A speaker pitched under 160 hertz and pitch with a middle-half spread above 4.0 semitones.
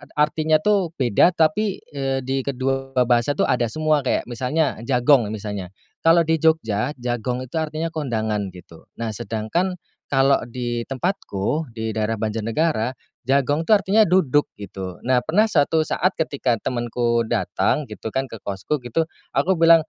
Yes: low, 135 Hz; wide, 5.5 semitones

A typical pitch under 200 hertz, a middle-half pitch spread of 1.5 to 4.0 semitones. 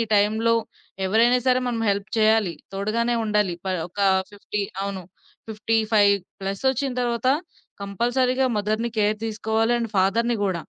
No: high, 215 Hz; narrow, 2.5 semitones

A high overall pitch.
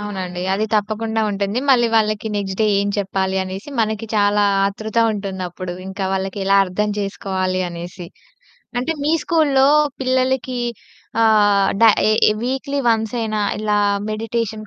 Yes: high, 210 Hz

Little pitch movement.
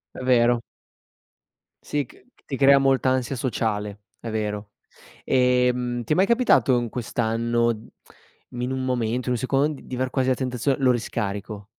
Yes: narrow, 2.1 semitones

